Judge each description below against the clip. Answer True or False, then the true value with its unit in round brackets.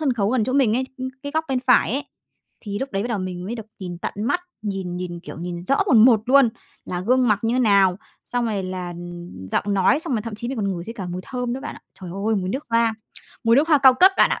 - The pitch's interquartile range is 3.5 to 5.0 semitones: False (5.5 semitones)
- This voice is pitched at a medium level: False (220 Hz)